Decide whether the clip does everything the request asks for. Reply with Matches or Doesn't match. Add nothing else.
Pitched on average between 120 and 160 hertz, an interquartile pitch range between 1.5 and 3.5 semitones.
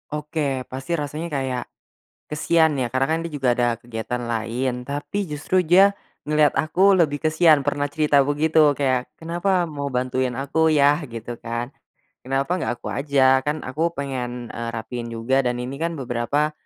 Doesn't match